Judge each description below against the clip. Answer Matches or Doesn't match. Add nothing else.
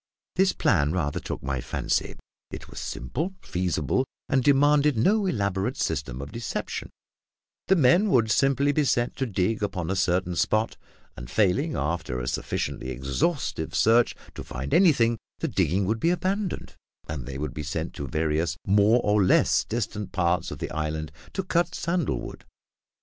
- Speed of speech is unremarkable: Matches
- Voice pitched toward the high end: Doesn't match